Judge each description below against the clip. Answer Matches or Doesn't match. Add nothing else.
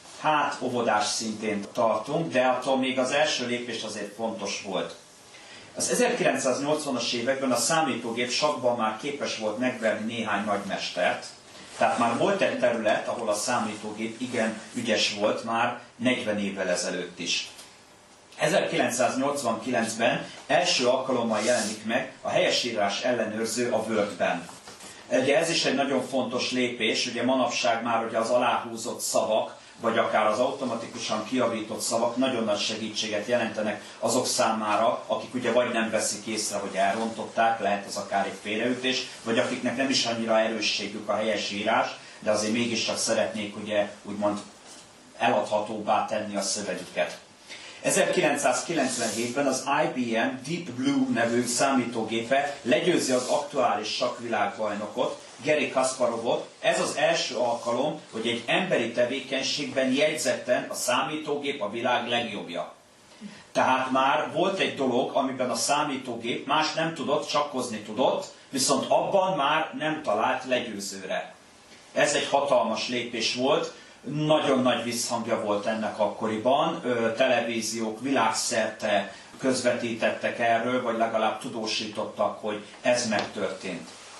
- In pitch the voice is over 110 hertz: Matches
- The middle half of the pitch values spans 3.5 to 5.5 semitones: Doesn't match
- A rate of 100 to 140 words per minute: Matches